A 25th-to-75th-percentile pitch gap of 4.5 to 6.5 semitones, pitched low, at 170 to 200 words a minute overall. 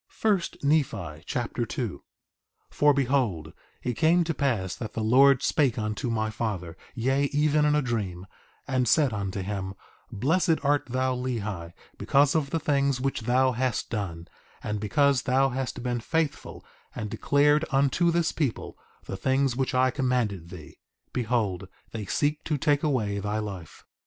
No: average, 5.1 semitones; low, 125 Hz; average, 160 wpm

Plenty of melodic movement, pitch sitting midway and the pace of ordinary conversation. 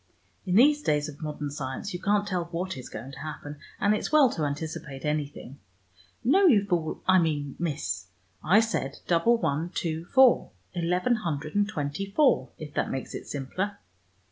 Yes: wide, 5.7 semitones; medium, 165 Hz; average, 175 wpm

